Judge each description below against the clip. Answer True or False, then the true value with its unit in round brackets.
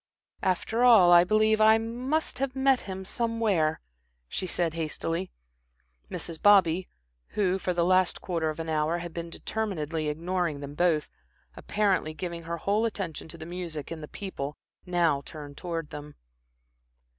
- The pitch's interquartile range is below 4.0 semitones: False (4.3 semitones)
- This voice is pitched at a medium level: True (175 Hz)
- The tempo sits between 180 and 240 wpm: False (155 wpm)